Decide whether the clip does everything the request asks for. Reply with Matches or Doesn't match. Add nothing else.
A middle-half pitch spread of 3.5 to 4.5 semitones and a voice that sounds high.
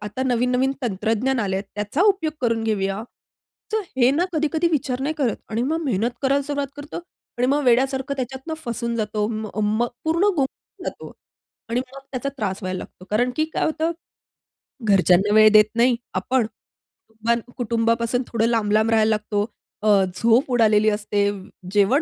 Matches